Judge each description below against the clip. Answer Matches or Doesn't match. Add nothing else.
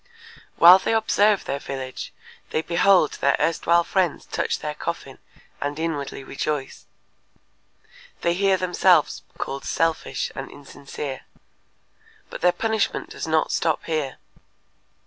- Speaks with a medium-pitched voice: Matches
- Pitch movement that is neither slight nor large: Matches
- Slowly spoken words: Matches